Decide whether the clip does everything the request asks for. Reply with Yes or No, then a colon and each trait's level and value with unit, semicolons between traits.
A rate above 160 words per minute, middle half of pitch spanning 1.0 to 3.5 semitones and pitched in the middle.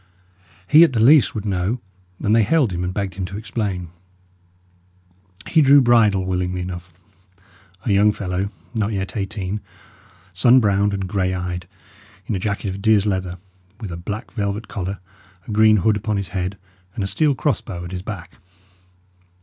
No: average, 175 wpm; average, 3.0 semitones; low, 100 Hz